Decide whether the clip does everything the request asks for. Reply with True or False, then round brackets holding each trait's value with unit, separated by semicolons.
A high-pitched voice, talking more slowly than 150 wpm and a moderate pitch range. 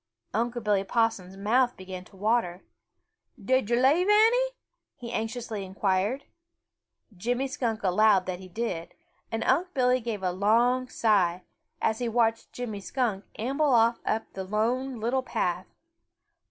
True (225 Hz; 140 wpm; 4.1 semitones)